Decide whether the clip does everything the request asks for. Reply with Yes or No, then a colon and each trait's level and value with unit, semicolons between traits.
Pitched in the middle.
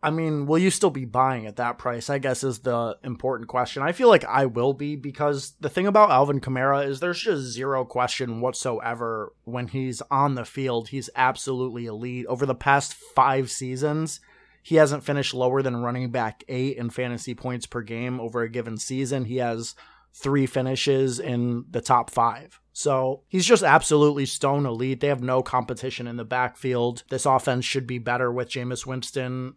No: low, 130 Hz